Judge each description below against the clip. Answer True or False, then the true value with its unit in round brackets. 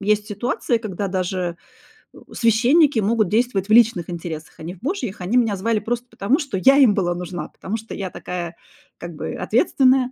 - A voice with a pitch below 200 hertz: False (210 Hz)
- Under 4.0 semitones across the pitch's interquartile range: False (5.0 semitones)